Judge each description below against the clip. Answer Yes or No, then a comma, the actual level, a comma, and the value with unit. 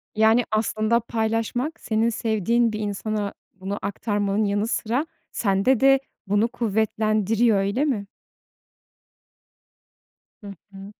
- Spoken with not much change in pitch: Yes, narrow, 2.3 semitones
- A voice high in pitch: Yes, high, 215 Hz